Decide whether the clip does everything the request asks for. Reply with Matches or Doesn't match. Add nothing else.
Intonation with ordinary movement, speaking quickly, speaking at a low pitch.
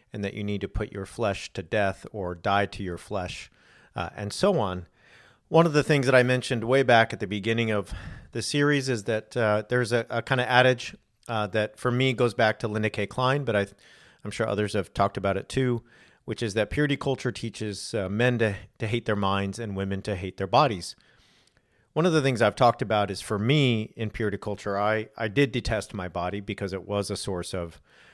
Matches